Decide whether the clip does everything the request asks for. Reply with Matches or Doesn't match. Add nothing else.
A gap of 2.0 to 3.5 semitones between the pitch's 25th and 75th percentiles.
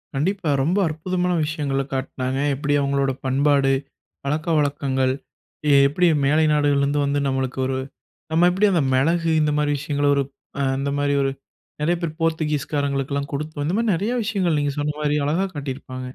Matches